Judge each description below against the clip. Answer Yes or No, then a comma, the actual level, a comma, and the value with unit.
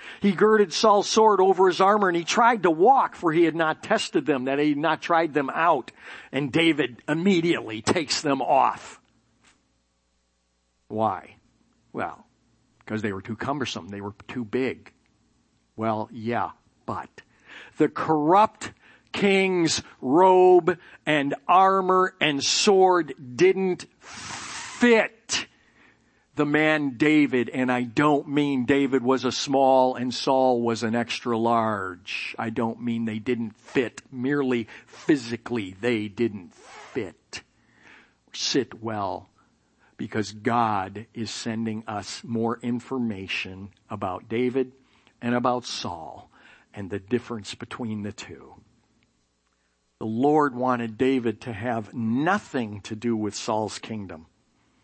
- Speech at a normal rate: No, slow, 125 wpm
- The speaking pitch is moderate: No, low, 125 Hz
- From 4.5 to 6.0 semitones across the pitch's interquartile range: Yes, wide, 5.5 semitones